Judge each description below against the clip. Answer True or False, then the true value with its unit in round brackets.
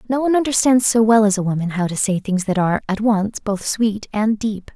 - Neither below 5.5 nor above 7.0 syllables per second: True (5.6 syllables/s)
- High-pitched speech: True (210 Hz)